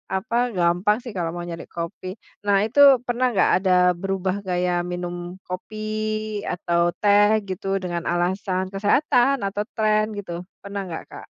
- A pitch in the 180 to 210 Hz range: Yes, high, 190 Hz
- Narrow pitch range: No, average, 3.0 semitones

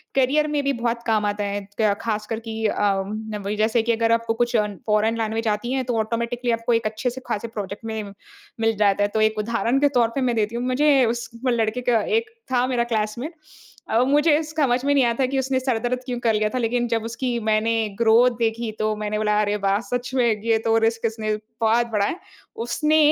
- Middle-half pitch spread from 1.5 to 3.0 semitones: Yes, narrow, 2.4 semitones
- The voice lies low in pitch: No, high, 230 Hz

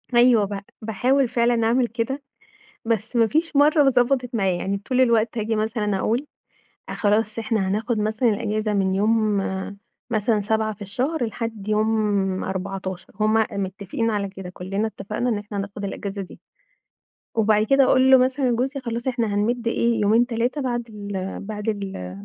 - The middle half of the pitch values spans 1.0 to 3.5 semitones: Yes, average, 2.9 semitones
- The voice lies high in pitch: Yes, high, 220 Hz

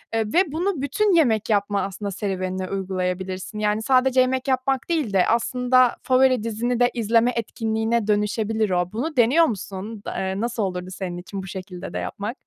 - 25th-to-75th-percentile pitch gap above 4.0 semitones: Yes, average, 4.6 semitones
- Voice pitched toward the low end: No, high, 220 Hz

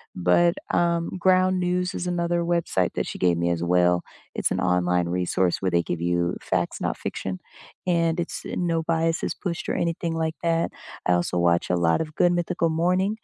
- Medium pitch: Yes, medium, 165 Hz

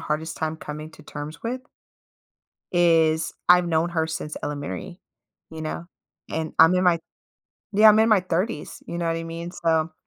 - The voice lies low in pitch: No, medium, 165 Hz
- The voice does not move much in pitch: Yes, narrow, 2.0 semitones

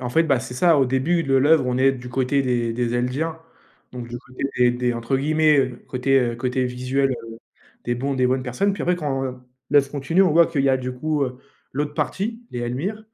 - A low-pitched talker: Yes, low, 130 Hz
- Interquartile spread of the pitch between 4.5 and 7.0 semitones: No, average, 3.2 semitones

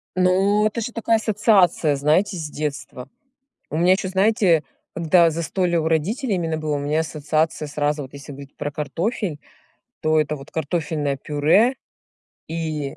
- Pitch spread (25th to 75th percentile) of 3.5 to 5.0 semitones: Yes, average, 4.1 semitones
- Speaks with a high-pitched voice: No, medium, 160 Hz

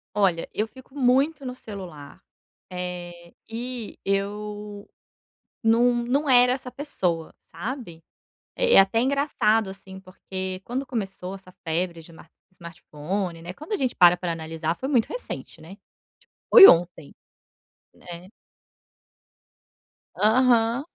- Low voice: No, high, 200 Hz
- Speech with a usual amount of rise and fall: No, wide, 6.0 semitones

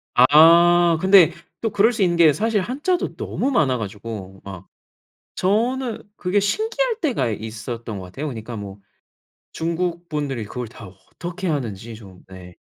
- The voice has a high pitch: No, medium, 155 Hz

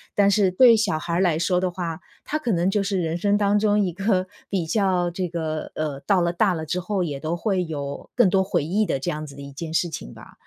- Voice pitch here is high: No, medium, 180 Hz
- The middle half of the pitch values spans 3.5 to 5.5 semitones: Yes, average, 3.9 semitones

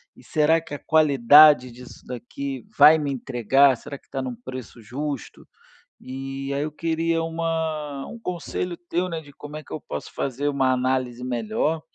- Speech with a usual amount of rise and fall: Yes, average, 3.4 semitones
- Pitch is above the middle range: No, medium, 140 Hz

